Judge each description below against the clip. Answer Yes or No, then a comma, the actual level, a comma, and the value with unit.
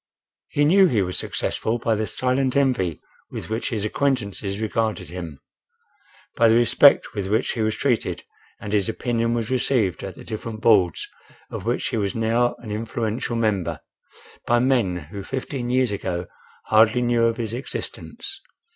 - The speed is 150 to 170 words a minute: Yes, average, 165 wpm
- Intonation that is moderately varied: Yes, average, 3.1 semitones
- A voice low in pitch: Yes, low, 115 Hz